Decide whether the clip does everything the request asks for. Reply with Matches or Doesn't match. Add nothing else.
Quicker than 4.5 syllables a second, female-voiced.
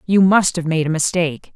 Matches